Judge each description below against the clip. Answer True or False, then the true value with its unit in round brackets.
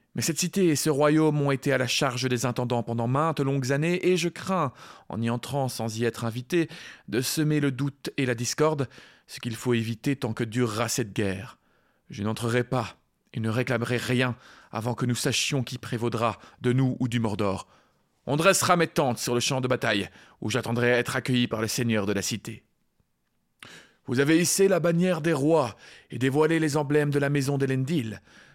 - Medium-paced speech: True (200 wpm)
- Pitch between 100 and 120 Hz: False (130 Hz)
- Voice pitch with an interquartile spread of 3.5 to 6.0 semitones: True (3.9 semitones)